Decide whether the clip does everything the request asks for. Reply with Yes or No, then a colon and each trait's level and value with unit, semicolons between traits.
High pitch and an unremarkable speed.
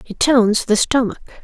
Yes: high, 235 Hz; average, 165 wpm